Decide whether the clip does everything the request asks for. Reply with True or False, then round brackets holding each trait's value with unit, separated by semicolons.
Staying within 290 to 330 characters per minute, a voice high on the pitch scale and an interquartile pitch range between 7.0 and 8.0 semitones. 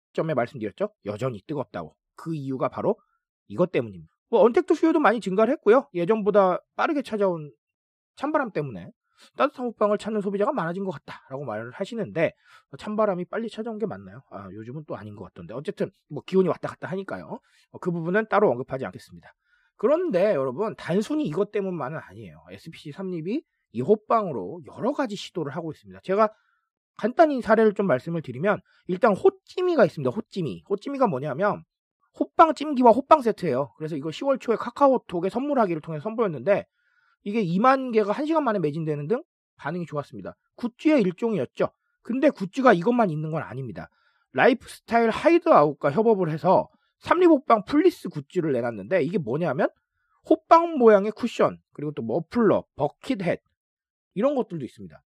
False (390 characters per minute; 205 Hz; 7.7 semitones)